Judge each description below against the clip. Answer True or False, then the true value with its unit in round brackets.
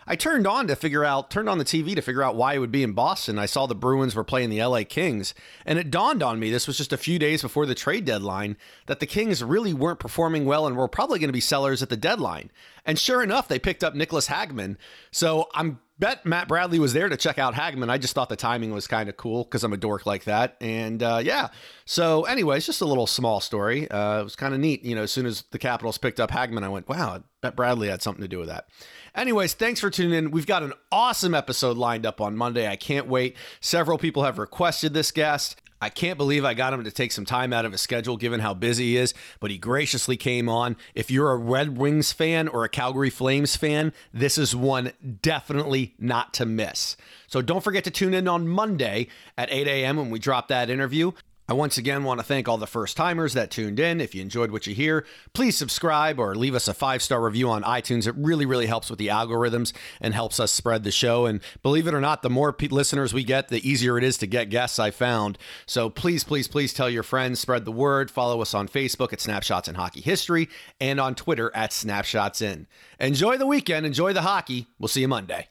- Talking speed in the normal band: False (245 wpm)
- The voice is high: False (130 Hz)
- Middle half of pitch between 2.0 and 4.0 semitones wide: False (4.5 semitones)